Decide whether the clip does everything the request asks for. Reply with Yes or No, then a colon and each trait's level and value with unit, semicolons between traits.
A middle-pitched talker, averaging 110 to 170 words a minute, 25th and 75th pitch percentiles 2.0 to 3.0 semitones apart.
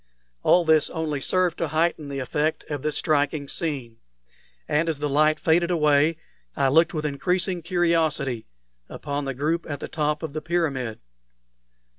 Yes: medium, 155 Hz; average, 160 wpm; narrow, 2.6 semitones